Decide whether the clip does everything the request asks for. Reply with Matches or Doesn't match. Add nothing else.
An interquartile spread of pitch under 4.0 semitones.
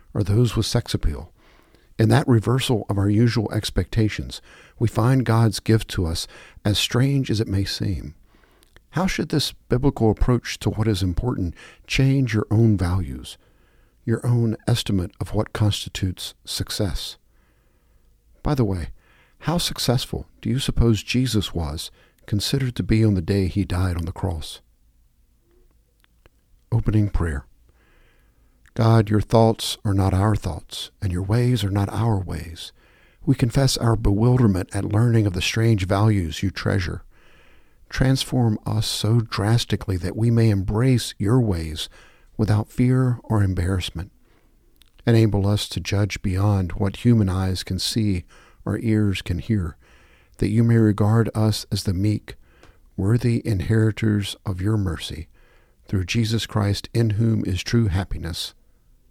Matches